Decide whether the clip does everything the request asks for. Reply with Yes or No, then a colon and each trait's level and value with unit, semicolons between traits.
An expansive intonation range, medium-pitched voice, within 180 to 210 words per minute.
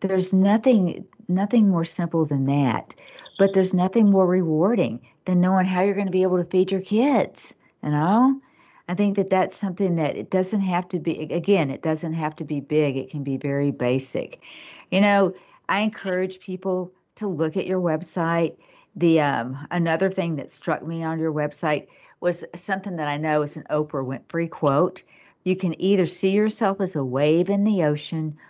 No: average, 3.8 semitones; medium, 180 Hz; average, 190 wpm